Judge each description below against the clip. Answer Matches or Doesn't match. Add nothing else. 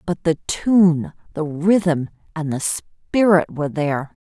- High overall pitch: Doesn't match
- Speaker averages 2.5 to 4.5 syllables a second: Matches